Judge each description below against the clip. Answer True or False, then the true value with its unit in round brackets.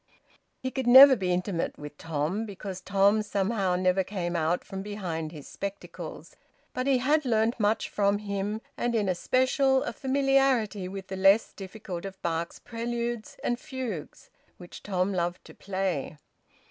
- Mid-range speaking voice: False (200 Hz)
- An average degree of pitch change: True (4.5 semitones)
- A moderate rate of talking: True (155 wpm)